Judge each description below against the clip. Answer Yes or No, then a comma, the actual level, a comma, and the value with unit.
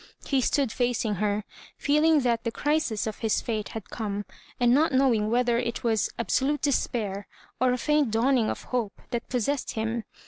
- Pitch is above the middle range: Yes, high, 240 Hz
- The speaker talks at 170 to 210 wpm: Yes, average, 180 wpm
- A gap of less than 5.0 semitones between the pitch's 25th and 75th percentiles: Yes, average, 3.4 semitones